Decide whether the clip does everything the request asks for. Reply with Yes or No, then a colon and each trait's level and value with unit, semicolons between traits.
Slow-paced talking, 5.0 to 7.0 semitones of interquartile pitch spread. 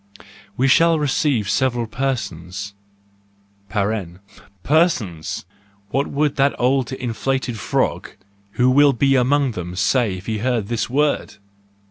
Yes: slow, 120 wpm; average, 5.3 semitones